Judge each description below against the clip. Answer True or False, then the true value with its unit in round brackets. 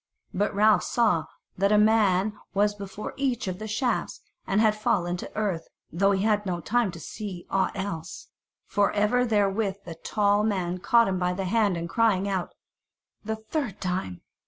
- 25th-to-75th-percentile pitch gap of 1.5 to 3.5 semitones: True (2.7 semitones)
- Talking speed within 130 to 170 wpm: False (180 wpm)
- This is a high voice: True (200 Hz)